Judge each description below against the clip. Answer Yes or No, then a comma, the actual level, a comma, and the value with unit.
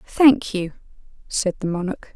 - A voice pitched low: No, high, 205 Hz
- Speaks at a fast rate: No, average, 140 wpm